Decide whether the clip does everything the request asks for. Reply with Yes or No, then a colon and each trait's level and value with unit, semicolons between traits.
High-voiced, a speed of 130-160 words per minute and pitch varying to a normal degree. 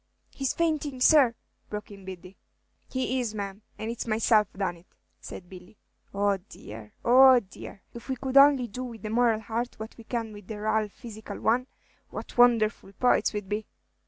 No: high, 220 Hz; average, 185 wpm; average, 3.4 semitones